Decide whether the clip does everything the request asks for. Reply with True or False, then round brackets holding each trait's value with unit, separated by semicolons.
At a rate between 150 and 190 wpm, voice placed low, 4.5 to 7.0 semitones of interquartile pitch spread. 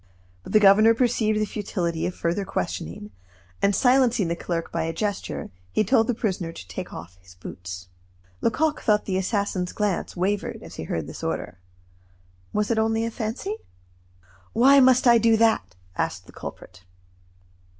False (165 wpm; 205 Hz; 5.4 semitones)